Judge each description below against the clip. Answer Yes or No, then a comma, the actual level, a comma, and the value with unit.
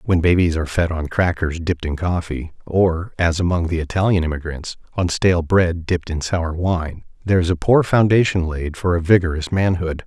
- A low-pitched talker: Yes, very low, 85 Hz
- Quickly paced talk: No, average, 190 wpm